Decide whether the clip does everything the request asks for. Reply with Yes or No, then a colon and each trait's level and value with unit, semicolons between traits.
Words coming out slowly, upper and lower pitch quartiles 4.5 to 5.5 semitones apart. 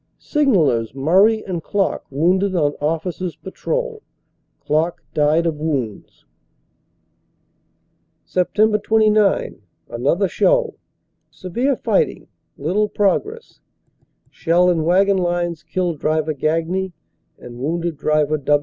Yes: slow, 100 wpm; average, 5.1 semitones